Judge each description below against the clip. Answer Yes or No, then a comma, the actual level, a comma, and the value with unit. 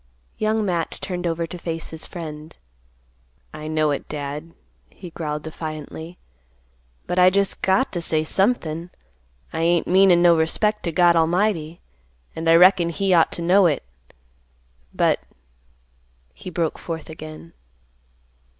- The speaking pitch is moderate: Yes, medium, 170 Hz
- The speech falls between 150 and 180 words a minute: No, average, 140 wpm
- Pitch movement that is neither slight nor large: No, narrow, 2.3 semitones